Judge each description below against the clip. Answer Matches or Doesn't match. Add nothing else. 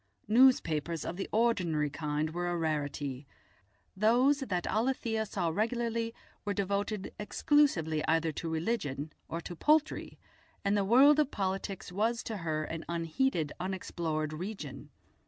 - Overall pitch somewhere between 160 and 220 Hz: Matches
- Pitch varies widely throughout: Matches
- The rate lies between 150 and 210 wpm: Doesn't match